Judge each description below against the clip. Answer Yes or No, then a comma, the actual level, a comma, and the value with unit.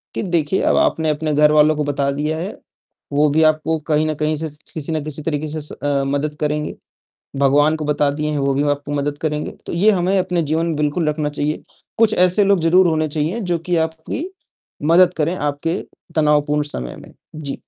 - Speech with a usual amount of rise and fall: No, narrow, 1.9 semitones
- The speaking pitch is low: No, medium, 155 Hz